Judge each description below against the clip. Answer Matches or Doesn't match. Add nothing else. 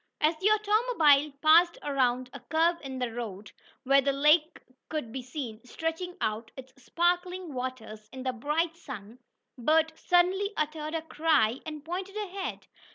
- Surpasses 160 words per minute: Doesn't match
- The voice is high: Matches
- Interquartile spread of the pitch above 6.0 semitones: Doesn't match